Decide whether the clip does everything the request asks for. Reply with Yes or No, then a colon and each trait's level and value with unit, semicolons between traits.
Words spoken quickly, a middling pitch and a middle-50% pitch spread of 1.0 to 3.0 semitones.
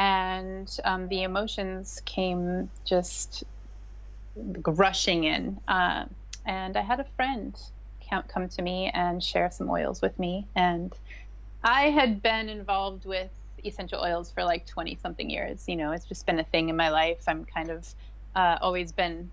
No: average, 160 wpm; medium, 180 Hz; narrow, 2.6 semitones